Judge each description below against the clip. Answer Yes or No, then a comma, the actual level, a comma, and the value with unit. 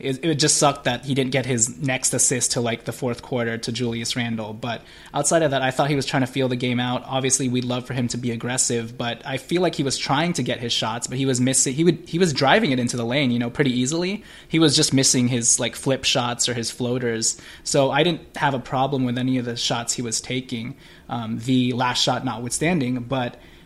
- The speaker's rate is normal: No, fast, 255 wpm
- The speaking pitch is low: Yes, low, 130 Hz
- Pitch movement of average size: No, narrow, 2.3 semitones